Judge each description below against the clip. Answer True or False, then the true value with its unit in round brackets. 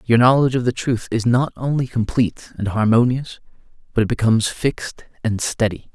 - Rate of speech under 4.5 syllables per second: False (5.6 syllables/s)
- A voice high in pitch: False (115 Hz)